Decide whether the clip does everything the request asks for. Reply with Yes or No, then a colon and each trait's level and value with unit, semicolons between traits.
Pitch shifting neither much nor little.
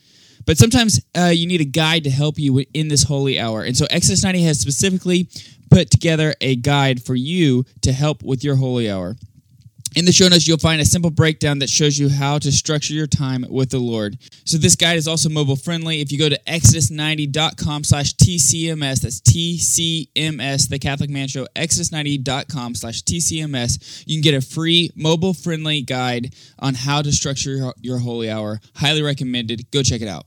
Yes: average, 3.5 semitones